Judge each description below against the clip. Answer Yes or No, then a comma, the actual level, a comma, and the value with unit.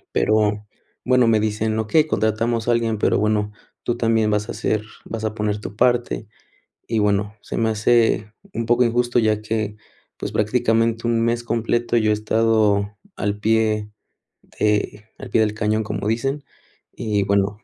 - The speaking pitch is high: No, low, 110 Hz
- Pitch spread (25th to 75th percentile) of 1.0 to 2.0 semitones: Yes, narrow, 1.6 semitones